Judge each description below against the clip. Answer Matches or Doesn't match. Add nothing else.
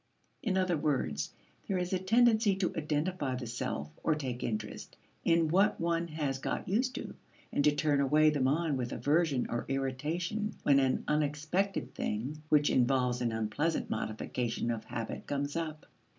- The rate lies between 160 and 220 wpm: Matches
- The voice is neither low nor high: Matches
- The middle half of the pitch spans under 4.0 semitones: Doesn't match